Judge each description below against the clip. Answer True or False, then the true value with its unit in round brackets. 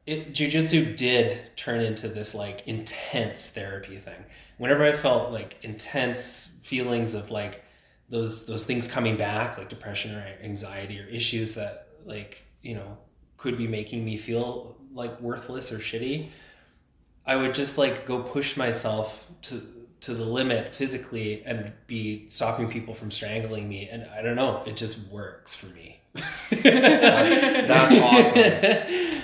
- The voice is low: True (115 Hz)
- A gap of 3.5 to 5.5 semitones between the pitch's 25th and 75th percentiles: False (3.1 semitones)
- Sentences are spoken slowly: False (150 wpm)